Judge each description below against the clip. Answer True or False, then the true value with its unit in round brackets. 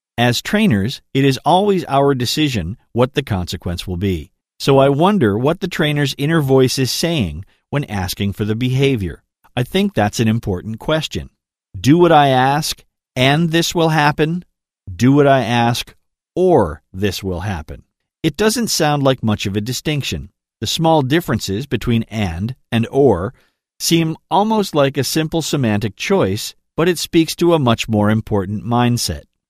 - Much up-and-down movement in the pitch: True (6.8 semitones)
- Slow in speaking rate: False (165 wpm)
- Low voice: True (130 Hz)